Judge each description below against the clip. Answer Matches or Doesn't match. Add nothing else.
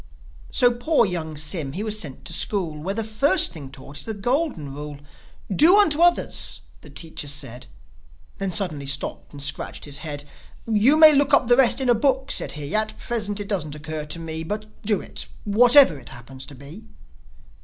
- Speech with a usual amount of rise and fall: Doesn't match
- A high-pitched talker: Matches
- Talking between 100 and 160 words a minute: Doesn't match